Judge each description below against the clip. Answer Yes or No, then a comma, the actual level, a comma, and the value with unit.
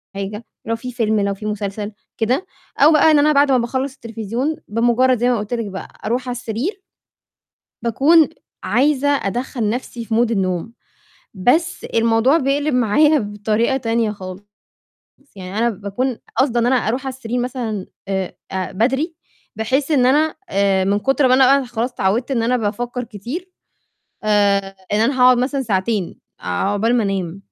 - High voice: Yes, high, 235 Hz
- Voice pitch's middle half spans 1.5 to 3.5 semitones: No, average, 4.1 semitones